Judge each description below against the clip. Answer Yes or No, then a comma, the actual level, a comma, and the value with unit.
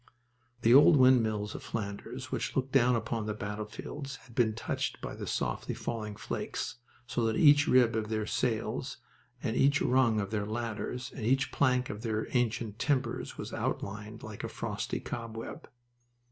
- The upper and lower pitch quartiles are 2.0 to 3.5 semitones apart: Yes, average, 2.9 semitones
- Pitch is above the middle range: No, low, 115 Hz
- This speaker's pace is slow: No, average, 165 wpm